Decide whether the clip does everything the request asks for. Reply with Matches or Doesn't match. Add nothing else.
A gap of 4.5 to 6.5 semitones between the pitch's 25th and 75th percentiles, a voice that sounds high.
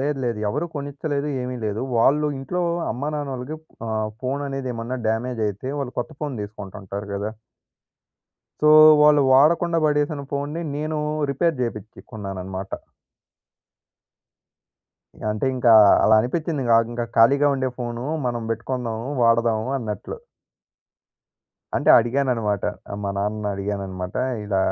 Doesn't match